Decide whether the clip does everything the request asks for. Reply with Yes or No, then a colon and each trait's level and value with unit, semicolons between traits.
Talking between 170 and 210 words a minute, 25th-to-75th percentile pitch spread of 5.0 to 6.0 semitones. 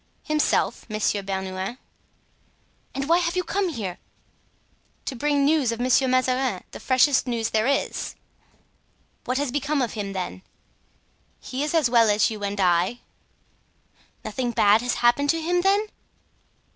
No: average, 145 wpm; wide, 5.4 semitones